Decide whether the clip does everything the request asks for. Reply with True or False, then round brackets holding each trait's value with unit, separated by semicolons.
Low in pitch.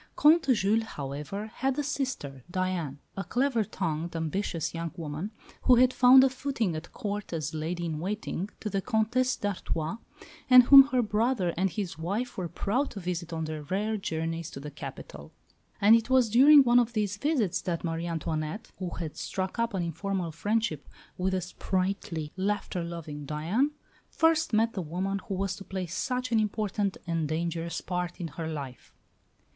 False (190 Hz)